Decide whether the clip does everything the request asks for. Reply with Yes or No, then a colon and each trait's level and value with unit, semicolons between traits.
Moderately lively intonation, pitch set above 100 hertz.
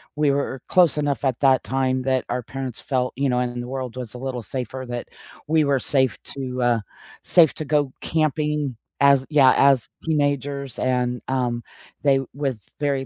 No: narrow, 2.1 semitones; low, 135 Hz